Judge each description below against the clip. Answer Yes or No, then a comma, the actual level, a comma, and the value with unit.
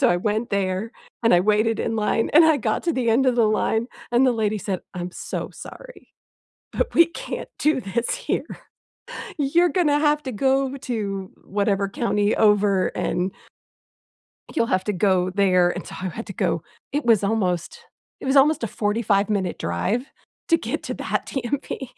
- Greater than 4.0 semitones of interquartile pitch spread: Yes, average, 5.2 semitones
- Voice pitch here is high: Yes, high, 220 Hz